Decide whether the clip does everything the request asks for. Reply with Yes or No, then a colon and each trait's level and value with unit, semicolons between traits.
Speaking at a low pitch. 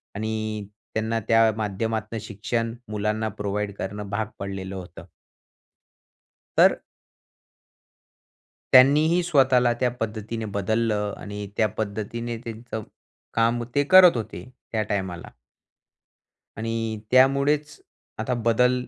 Yes: low, 110 Hz